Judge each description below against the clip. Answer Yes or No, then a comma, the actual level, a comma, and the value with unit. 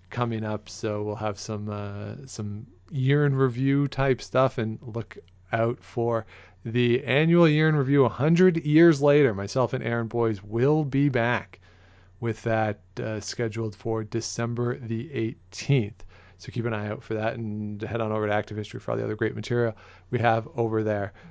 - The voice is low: Yes, low, 115 Hz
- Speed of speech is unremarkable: Yes, average, 180 wpm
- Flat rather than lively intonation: No, average, 3.3 semitones